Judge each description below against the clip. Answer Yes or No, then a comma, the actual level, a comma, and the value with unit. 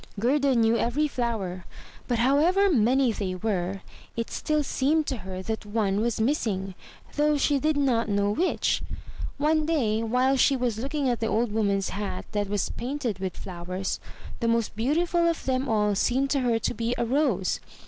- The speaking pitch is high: Yes, high, 235 Hz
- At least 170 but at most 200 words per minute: Yes, average, 180 wpm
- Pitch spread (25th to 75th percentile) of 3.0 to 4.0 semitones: No, average, 5.1 semitones